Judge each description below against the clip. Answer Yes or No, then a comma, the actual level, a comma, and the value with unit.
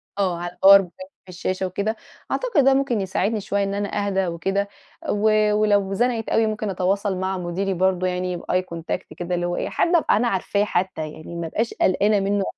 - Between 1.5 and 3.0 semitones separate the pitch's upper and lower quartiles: Yes, narrow, 2.6 semitones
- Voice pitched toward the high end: Yes, high, 195 Hz